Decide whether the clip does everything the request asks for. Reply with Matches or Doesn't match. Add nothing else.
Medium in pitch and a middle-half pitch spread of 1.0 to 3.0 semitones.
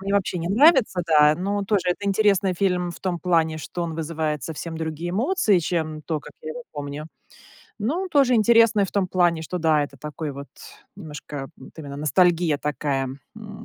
Doesn't match